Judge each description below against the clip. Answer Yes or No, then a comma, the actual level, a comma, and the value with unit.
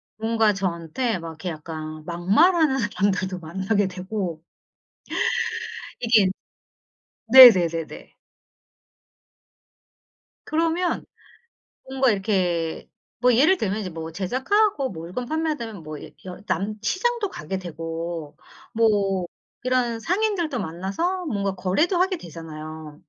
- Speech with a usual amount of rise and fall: No, wide, 7.5 semitones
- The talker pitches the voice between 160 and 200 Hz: Yes, high, 195 Hz